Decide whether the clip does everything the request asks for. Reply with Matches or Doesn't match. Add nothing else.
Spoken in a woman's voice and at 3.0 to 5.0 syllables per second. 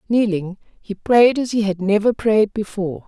Matches